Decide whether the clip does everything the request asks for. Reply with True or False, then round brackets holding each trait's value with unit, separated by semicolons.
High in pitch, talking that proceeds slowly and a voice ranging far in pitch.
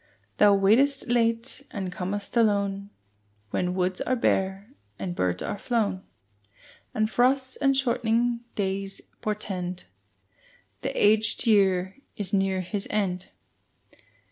False (205 Hz; 115 wpm; 3.3 semitones)